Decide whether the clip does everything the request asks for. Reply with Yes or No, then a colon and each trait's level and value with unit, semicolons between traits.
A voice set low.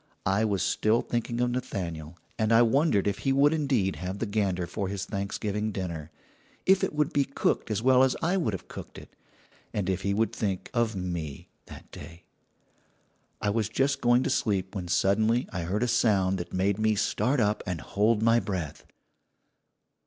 Yes: low, 105 Hz